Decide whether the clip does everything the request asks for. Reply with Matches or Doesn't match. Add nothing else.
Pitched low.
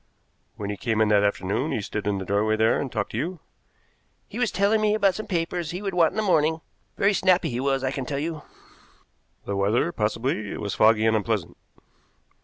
Matches